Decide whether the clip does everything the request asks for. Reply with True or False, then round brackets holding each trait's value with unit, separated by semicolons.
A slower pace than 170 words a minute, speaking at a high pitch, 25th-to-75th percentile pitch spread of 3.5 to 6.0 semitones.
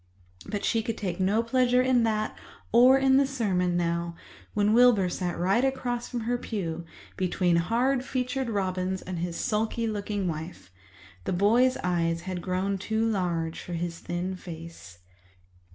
True (155 wpm; 200 Hz; 5.2 semitones)